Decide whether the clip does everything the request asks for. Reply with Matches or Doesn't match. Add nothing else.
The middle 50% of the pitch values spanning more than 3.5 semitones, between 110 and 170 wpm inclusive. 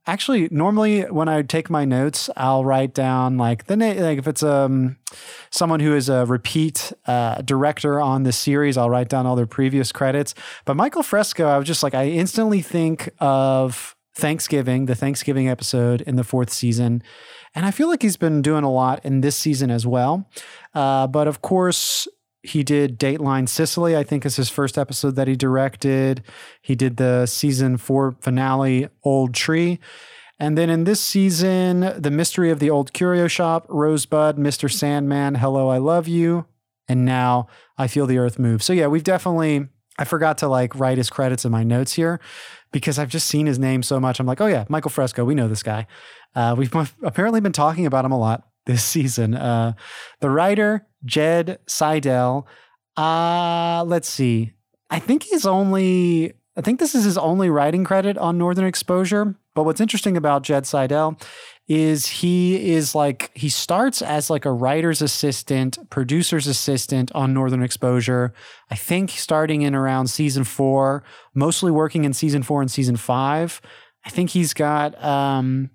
Doesn't match